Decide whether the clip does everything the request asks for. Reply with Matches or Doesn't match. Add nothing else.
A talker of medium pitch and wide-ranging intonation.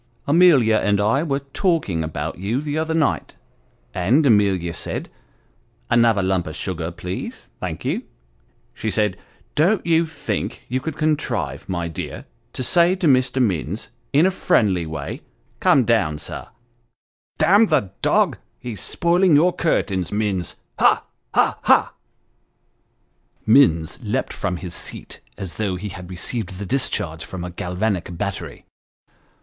Doesn't match